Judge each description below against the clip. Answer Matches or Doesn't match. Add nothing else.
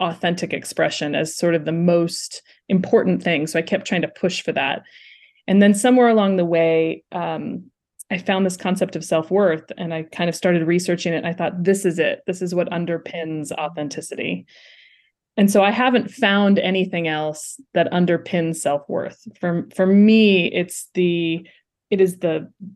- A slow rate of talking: Doesn't match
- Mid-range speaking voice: Matches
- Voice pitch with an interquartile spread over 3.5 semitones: Doesn't match